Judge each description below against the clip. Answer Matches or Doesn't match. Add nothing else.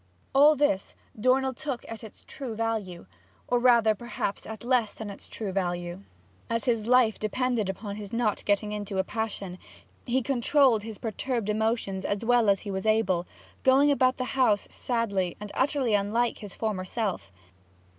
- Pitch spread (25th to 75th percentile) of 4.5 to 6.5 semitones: Doesn't match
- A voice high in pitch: Matches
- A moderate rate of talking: Matches